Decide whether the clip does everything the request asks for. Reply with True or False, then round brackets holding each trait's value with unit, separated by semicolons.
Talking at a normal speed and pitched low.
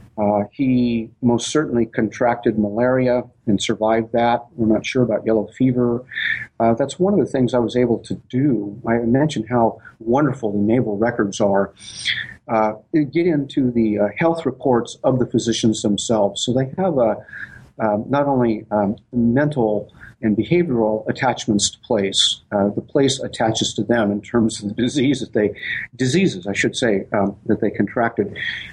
True (175 wpm; 115 Hz)